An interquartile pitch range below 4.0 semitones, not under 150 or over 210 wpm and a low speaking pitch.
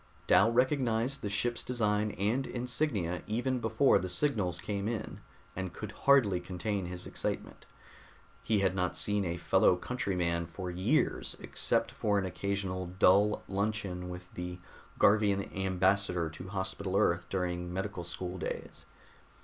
No: average, 3.1 semitones; average, 140 wpm; very low, 95 Hz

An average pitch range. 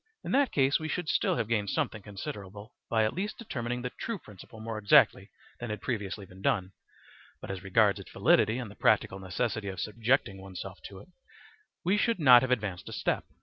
Yes: average, 4.5 semitones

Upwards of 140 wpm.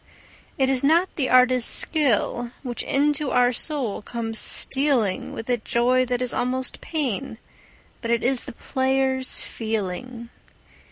No: slow, 135 wpm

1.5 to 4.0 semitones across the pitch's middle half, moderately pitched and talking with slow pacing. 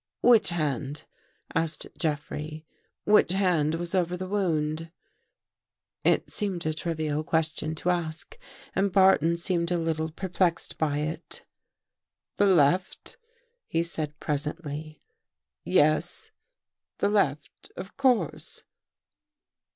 Yes: average, 2.8 semitones; medium, 165 Hz; slow, 115 wpm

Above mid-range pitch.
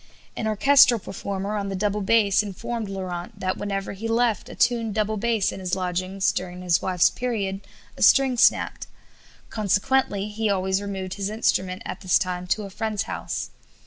Yes: high, 200 Hz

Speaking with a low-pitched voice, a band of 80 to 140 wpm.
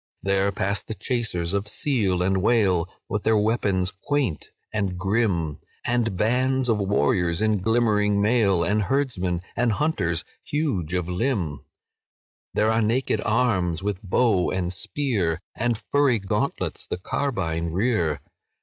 Yes: low, 105 Hz; slow, 135 wpm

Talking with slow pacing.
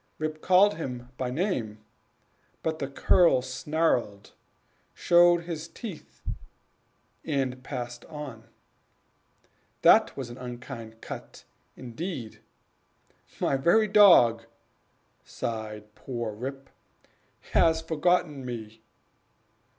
Yes: slow, 90 wpm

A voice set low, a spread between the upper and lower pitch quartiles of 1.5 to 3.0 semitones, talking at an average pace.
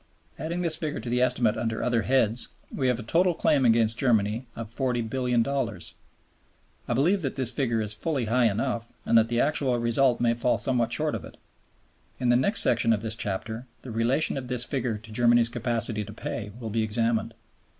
Yes: low, 120 Hz; narrow, 2.5 semitones; average, 195 wpm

